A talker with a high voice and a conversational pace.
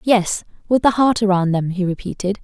Yes: high, 200 Hz; average, 195 wpm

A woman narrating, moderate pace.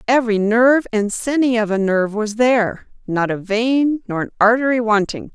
Yes: female; average, 170 wpm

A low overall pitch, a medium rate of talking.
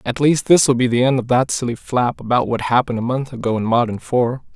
No: low, 125 Hz; fast, 250 wpm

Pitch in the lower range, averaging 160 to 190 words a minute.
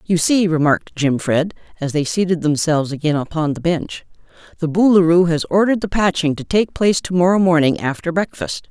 No: medium, 170 Hz; average, 180 wpm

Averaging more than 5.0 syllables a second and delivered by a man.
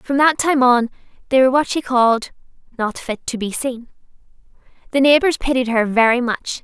No: 5.3 syllables/s; female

